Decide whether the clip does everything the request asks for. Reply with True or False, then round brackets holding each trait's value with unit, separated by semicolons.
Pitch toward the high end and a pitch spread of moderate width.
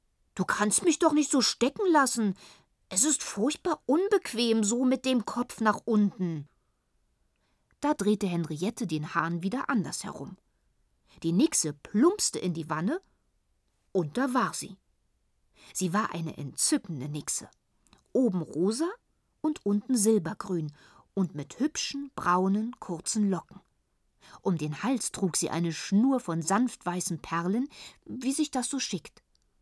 False (210 Hz; 7.0 semitones)